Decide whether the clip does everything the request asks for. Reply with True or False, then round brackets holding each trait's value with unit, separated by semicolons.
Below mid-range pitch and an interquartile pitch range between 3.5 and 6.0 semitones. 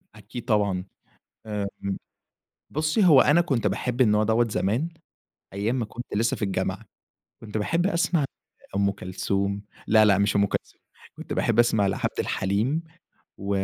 True (105 Hz; 4.2 semitones)